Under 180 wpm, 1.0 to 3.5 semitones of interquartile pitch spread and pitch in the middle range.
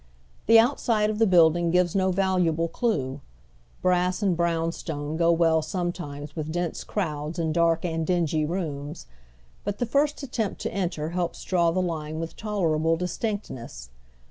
Yes: average, 155 wpm; average, 3.0 semitones; medium, 170 Hz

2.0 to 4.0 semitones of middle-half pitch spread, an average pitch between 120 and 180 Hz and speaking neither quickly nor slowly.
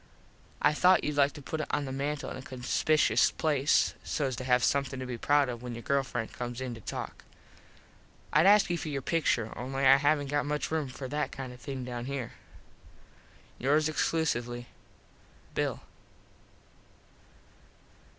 Yes: average, 3.0 semitones; low, 135 Hz; average, 170 wpm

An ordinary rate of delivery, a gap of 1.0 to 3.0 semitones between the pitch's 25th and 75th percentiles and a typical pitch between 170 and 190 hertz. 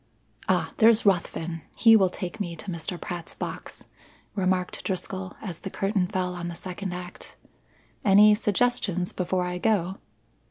Yes: average, 150 wpm; narrow, 2.4 semitones; medium, 185 Hz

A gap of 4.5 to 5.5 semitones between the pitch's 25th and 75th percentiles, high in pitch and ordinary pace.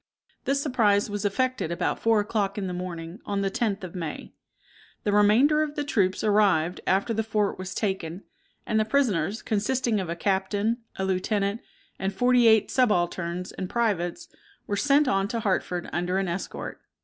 No: average, 3.5 semitones; high, 200 Hz; average, 175 wpm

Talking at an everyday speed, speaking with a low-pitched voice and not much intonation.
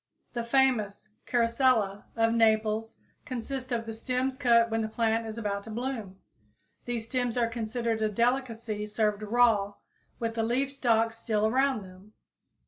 No: average, 155 wpm; high, 230 Hz; narrow, 2.1 semitones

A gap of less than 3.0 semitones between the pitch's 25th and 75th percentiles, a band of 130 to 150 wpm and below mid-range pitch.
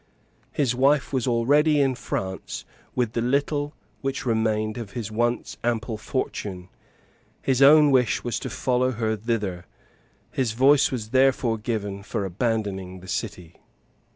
No: average, 3.7 semitones; average, 140 wpm; low, 115 Hz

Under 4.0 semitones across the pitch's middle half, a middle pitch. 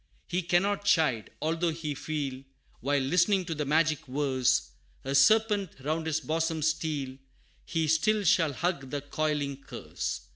Yes: average, 3.4 semitones; medium, 155 Hz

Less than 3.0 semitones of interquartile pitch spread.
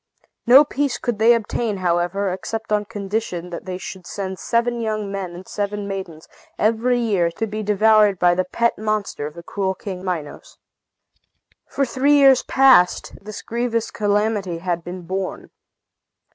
No: average, 3.7 semitones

